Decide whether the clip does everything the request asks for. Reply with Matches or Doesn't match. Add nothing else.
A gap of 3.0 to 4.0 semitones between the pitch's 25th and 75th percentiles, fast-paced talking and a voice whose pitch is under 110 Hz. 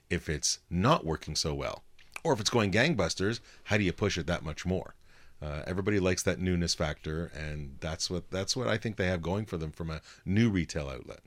Matches